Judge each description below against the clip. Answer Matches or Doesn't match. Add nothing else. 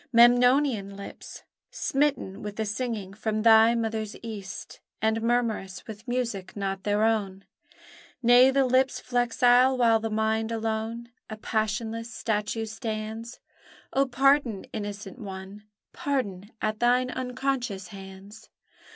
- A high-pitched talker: Matches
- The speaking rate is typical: Doesn't match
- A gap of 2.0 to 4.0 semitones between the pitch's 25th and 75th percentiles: Matches